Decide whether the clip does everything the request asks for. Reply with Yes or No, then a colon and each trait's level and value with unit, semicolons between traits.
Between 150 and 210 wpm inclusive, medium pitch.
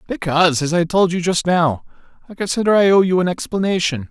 Yes: fast, 205 wpm; medium, 175 Hz